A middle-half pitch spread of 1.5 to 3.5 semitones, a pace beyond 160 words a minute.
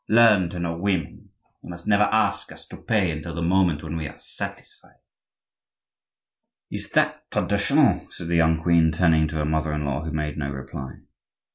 Yes: narrow, 2.5 semitones; average, 180 wpm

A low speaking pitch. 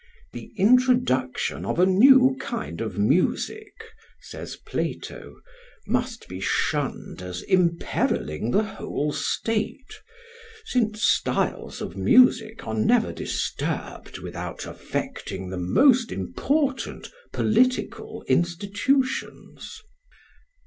No: high, 215 Hz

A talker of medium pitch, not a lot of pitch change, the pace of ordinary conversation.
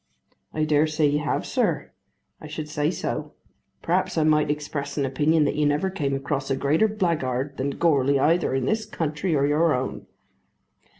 Yes: medium, 150 Hz; narrow, 2.0 semitones; average, 180 wpm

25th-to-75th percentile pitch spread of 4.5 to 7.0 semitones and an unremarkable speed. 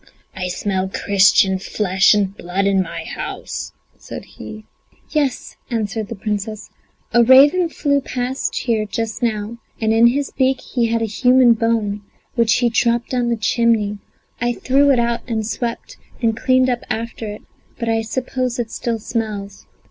No: average, 2.9 semitones; average, 165 wpm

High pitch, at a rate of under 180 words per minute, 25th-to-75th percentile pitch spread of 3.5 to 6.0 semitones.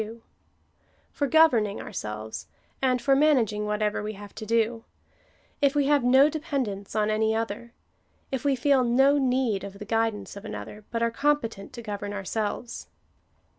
Yes: high, 230 Hz; average, 170 wpm; average, 4.3 semitones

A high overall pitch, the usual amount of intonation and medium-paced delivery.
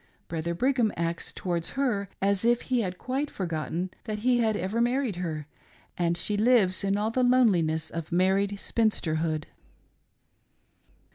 No: high, 200 Hz; wide, 5.7 semitones; average, 150 wpm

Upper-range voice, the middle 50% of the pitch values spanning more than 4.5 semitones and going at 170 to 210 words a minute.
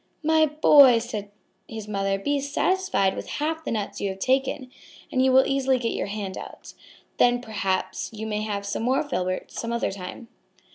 Yes: high, 235 Hz; average, 5.1 semitones; average, 185 wpm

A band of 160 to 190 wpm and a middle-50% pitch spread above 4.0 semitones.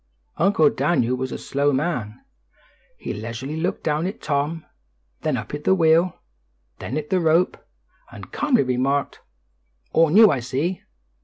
No: average, 150 wpm; average, 4.4 semitones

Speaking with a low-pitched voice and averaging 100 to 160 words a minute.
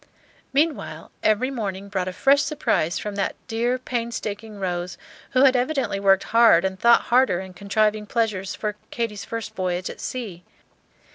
No: high, 215 Hz; average, 155 wpm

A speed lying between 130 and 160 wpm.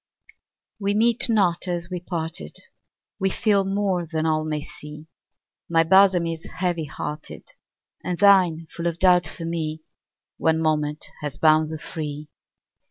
Yes: average, 145 wpm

